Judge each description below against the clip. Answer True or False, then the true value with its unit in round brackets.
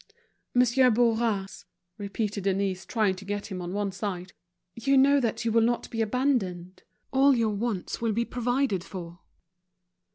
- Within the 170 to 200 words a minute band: False (155 wpm)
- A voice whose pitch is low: False (220 Hz)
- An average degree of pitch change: True (3.9 semitones)